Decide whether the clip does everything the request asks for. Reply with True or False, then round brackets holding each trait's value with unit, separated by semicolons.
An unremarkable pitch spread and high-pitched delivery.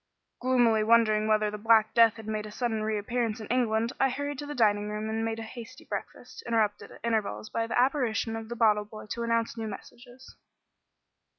False (1.7 semitones; 225 Hz)